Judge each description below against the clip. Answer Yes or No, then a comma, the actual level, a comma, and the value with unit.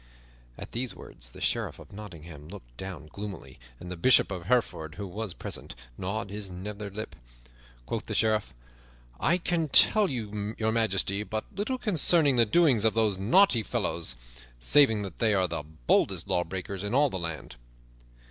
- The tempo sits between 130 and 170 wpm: Yes, average, 165 wpm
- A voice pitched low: Yes, low, 105 Hz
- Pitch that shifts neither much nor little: Yes, average, 4.5 semitones